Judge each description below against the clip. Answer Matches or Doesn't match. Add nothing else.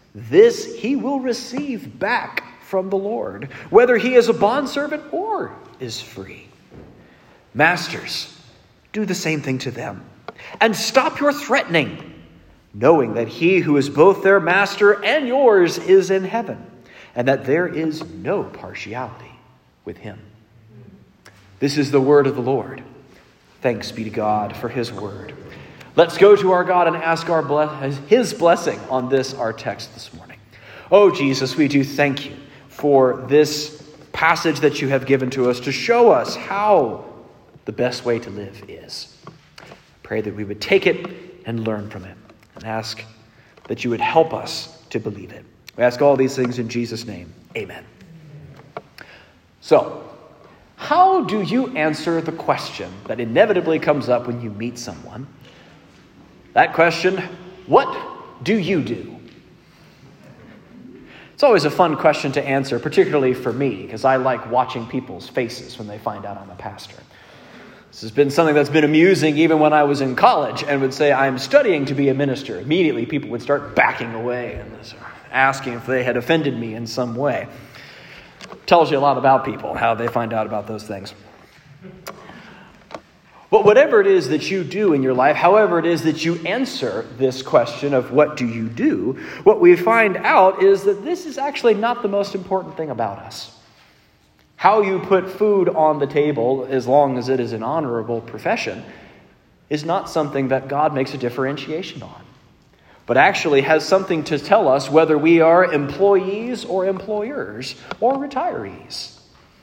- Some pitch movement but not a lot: Doesn't match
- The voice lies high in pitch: Doesn't match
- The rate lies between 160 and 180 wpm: Matches